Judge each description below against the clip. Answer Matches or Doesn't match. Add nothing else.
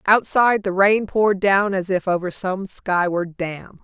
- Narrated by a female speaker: Matches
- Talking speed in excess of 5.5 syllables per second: Doesn't match